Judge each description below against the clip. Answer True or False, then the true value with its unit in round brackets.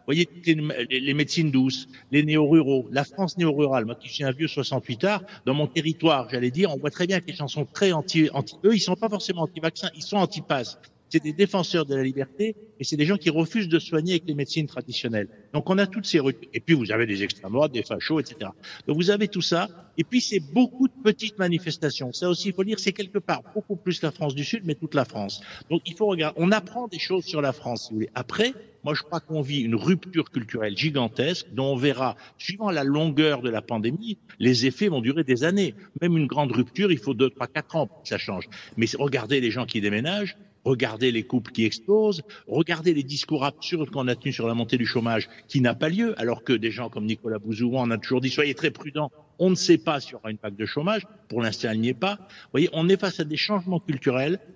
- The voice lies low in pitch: False (150 Hz)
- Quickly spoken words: True (245 wpm)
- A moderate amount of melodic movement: False (5.7 semitones)